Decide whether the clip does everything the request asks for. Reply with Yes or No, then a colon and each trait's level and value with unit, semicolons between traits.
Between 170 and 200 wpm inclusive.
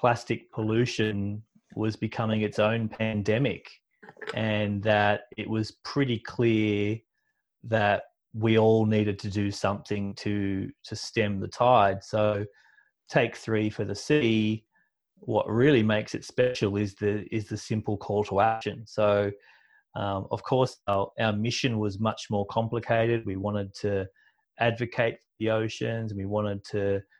No: average, 145 wpm